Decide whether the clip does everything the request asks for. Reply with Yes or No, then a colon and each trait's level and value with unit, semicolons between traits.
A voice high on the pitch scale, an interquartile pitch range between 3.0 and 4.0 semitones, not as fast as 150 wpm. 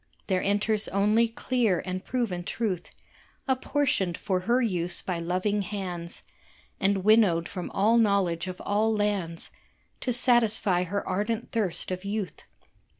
Yes: high, 200 Hz; average, 3.5 semitones; slow, 135 wpm